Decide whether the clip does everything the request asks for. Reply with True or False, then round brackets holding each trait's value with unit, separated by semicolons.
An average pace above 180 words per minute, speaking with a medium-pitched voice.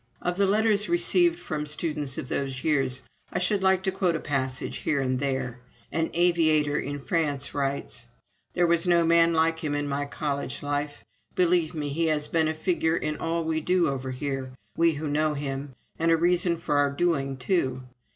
True (190 wpm; 155 Hz)